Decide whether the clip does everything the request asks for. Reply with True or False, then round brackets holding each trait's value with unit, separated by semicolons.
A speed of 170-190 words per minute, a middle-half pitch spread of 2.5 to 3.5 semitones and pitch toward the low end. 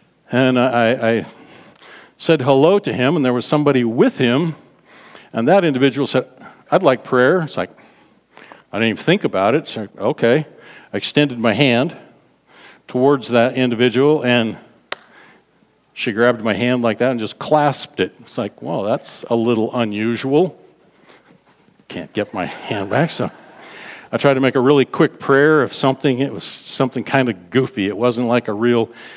True (175 wpm; 2.8 semitones; 125 Hz)